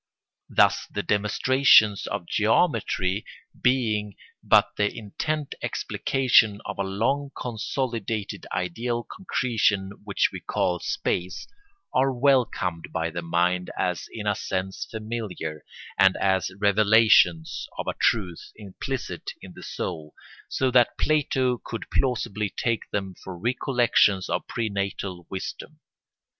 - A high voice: No, low, 105 Hz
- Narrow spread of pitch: No, average, 4.3 semitones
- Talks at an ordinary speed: No, slow, 120 wpm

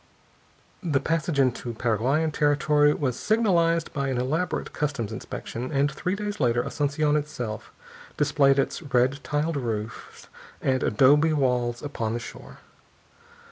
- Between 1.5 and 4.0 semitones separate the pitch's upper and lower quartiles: Yes, average, 3.5 semitones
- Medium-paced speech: No, slow, 130 wpm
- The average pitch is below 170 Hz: Yes, medium, 140 Hz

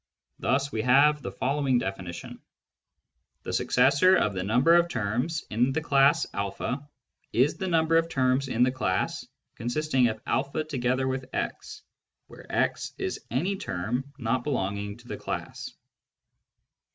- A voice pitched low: Yes, low, 130 Hz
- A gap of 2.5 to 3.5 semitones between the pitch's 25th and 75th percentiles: No, average, 4.5 semitones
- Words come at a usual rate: Yes, average, 150 wpm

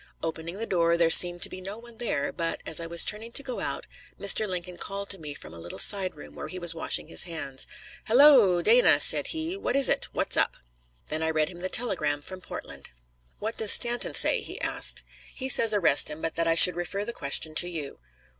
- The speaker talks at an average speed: No, fast, 230 wpm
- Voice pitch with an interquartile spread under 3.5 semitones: No, average, 5.1 semitones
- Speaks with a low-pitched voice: No, medium, 180 Hz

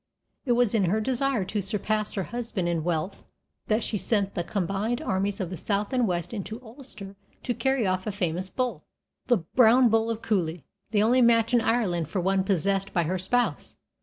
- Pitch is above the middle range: Yes, high, 205 Hz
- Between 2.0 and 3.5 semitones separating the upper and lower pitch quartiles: No, average, 3.9 semitones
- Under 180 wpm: No, average, 195 wpm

